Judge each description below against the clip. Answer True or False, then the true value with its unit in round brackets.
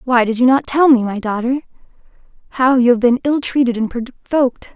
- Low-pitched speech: False (250 Hz)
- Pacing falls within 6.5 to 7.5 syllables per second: True (6.7 syllables/s)